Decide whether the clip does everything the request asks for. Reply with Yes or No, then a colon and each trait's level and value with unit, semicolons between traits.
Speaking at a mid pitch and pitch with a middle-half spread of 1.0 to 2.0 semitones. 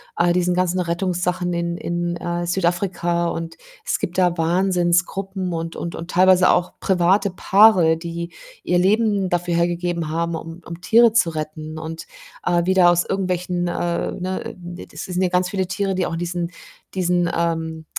Yes: medium, 175 Hz; narrow, 1.4 semitones